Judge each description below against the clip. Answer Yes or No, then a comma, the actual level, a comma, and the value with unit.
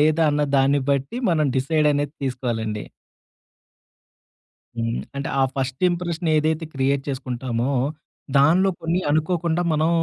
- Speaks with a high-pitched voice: No, medium, 145 Hz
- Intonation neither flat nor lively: Yes, average, 3.4 semitones